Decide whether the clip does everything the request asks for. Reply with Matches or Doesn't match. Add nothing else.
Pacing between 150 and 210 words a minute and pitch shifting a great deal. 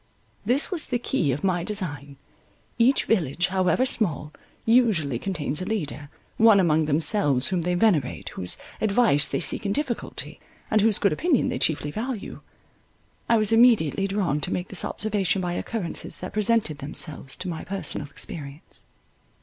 Matches